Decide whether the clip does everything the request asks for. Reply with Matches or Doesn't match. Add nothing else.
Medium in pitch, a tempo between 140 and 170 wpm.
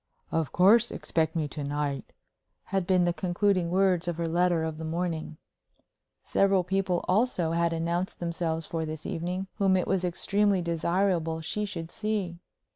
Matches